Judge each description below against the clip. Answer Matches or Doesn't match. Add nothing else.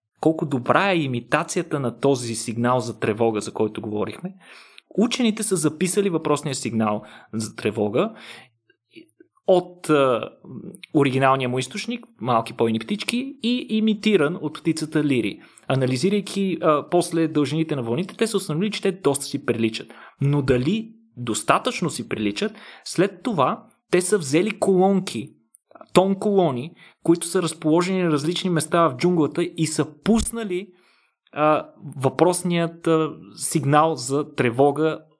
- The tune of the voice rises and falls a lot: Matches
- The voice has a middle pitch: Matches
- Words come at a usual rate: Matches